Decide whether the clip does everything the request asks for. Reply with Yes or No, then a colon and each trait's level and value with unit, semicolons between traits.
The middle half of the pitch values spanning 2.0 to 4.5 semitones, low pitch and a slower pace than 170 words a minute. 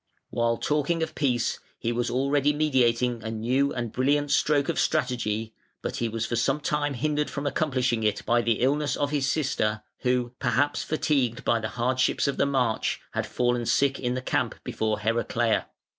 No: average, 3.4 semitones; low, 125 Hz; average, 180 wpm